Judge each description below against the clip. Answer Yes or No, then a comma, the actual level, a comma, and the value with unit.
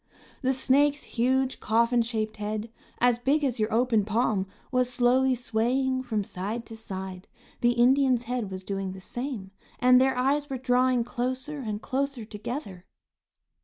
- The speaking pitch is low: No, high, 245 Hz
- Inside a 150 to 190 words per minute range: Yes, average, 155 wpm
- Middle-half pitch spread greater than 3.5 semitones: No, average, 3.2 semitones